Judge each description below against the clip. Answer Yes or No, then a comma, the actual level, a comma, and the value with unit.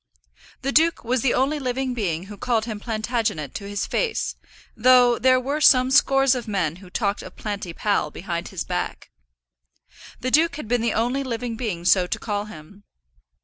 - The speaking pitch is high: Yes, high, 230 Hz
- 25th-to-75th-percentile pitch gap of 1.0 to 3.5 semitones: No, average, 4.2 semitones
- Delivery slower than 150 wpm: No, average, 185 wpm